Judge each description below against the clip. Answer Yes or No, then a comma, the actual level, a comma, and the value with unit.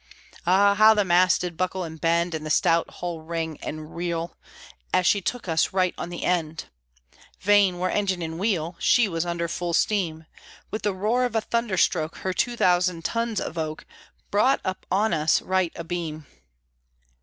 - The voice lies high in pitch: No, medium, 175 Hz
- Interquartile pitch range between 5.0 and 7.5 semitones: No, average, 3.4 semitones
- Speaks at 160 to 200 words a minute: Yes, average, 180 wpm